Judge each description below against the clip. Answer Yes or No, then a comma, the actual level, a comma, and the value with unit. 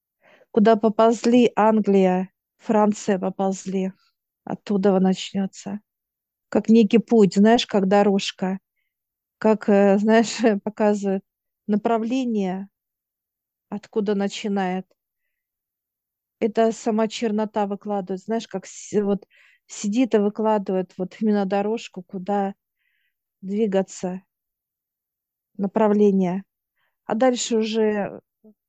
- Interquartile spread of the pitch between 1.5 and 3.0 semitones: Yes, narrow, 2.4 semitones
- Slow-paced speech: Yes, slow, 80 wpm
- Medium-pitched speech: No, high, 210 Hz